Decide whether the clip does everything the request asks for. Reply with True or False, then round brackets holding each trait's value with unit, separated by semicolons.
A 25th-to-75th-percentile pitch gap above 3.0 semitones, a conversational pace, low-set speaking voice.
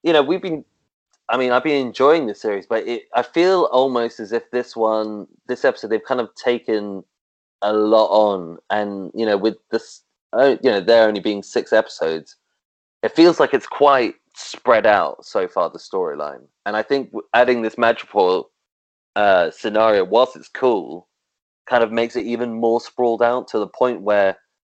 True (4.6 semitones; 180 wpm; 120 Hz)